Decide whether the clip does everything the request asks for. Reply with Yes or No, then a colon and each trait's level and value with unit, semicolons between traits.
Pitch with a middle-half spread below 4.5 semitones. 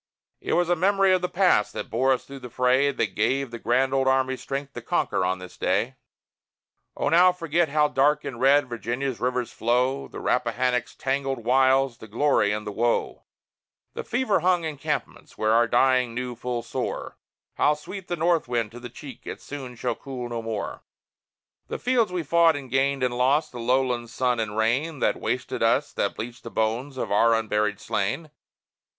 Yes: average, 3.6 semitones